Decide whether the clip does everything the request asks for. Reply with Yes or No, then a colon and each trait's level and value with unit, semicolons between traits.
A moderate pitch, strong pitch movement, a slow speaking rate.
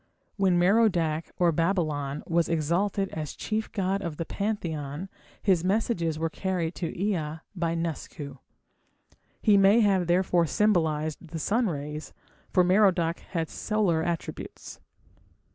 No: medium, 170 Hz; average, 3.4 semitones; slow, 125 wpm